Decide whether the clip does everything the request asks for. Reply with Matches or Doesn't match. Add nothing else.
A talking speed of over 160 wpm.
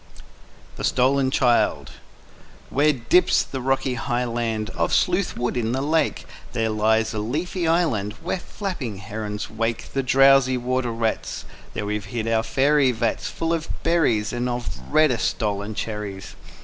Doesn't match